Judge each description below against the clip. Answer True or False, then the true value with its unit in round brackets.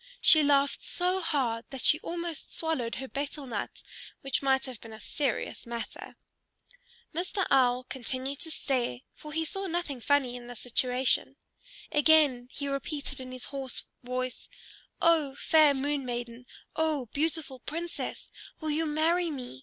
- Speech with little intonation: False (3.8 semitones)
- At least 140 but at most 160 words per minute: True (150 wpm)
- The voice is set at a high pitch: True (275 Hz)